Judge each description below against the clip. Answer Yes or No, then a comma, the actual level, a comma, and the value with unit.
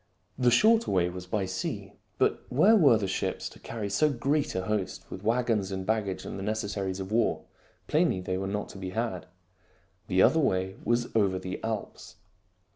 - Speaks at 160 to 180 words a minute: No, average, 190 wpm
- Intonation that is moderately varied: Yes, average, 4.0 semitones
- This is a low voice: Yes, low, 100 Hz